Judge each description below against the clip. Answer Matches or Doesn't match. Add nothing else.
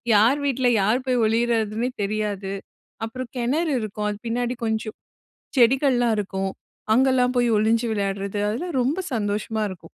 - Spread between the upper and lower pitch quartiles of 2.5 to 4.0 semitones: Matches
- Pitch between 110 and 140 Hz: Doesn't match